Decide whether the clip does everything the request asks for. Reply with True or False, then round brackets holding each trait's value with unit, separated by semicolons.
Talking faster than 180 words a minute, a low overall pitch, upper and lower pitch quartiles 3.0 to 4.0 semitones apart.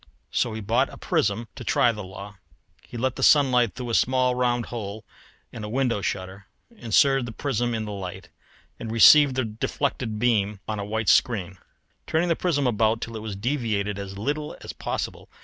True (190 wpm; 115 Hz; 3.6 semitones)